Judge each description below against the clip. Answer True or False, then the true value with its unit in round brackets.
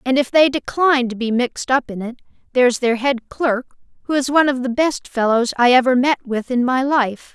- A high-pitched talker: True (255 Hz)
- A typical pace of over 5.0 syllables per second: True (5.4 syllables/s)